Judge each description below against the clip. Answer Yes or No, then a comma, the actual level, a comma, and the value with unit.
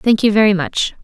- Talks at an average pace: No, fast, 230 wpm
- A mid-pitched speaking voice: No, high, 210 Hz